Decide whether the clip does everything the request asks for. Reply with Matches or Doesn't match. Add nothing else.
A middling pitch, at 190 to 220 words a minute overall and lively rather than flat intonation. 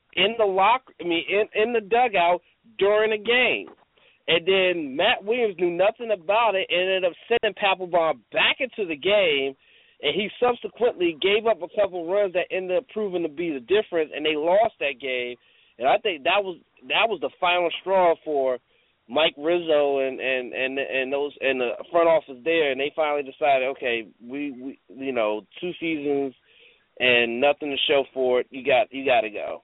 Matches